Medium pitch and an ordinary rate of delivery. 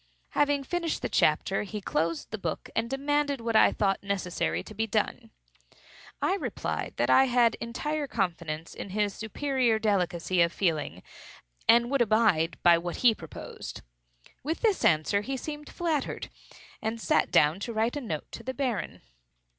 No: high, 220 Hz; average, 160 wpm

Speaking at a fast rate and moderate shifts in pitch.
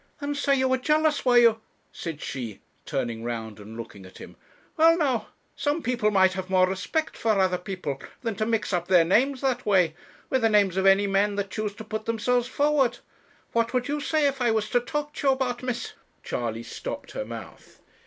No: fast, 215 wpm; wide, 5.9 semitones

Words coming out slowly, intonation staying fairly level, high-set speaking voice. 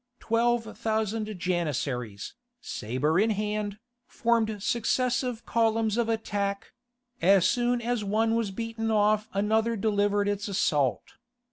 Yes: slow, 115 wpm; narrow, 2.3 semitones; high, 215 Hz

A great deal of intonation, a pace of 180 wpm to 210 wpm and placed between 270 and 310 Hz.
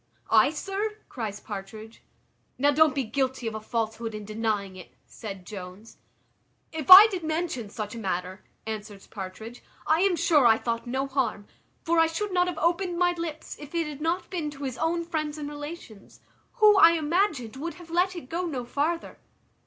Yes: wide, 7.4 semitones; average, 185 wpm; very high, 285 Hz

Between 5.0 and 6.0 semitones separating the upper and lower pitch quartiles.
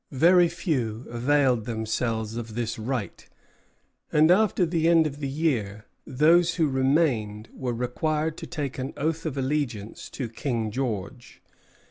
Yes: wide, 5.4 semitones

